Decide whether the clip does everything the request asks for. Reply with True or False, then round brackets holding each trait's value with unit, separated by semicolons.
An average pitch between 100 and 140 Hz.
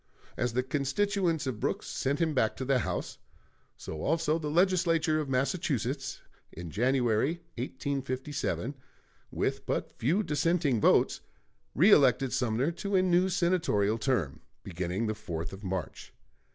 True (135 Hz)